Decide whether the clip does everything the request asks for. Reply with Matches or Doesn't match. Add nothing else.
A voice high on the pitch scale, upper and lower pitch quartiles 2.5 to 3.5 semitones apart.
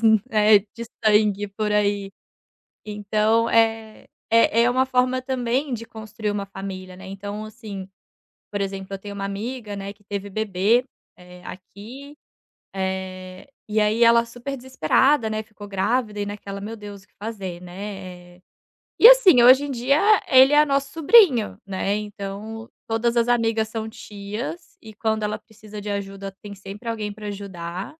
Matches